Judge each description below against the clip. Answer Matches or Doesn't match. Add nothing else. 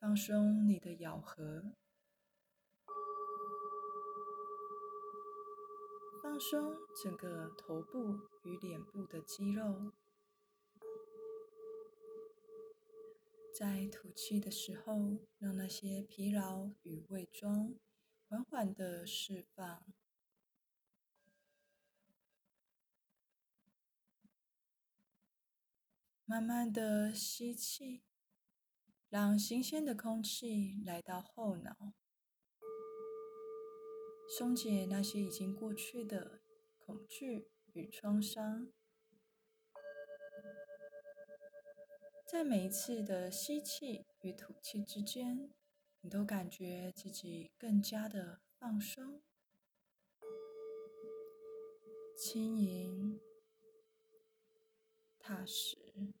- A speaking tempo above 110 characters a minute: Doesn't match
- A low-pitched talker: Doesn't match